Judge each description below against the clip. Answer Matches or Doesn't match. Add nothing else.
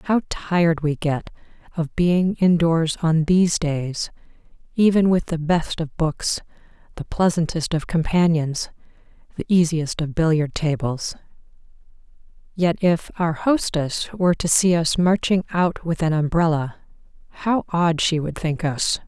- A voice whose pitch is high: Doesn't match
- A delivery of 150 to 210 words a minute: Doesn't match